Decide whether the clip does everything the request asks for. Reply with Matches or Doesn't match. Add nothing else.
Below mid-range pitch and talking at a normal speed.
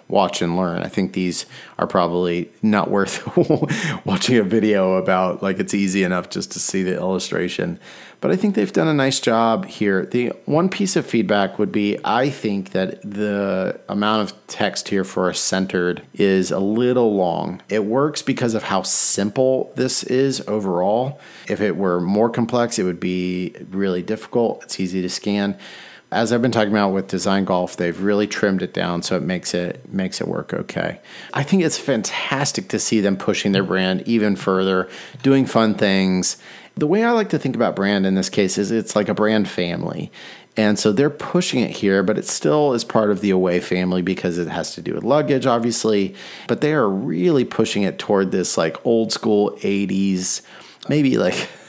Matches